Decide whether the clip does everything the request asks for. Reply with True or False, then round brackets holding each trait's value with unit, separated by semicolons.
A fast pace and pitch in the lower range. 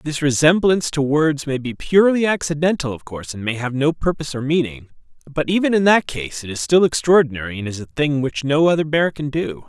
False (225 wpm; 145 Hz)